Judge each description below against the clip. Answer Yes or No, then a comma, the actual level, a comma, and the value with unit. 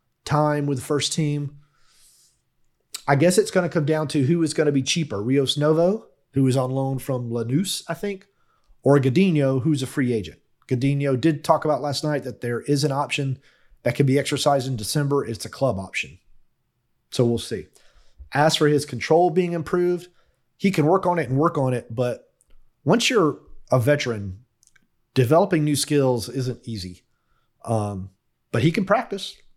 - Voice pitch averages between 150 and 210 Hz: No, medium, 140 Hz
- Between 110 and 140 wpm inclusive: No, average, 180 wpm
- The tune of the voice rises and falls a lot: No, average, 3.8 semitones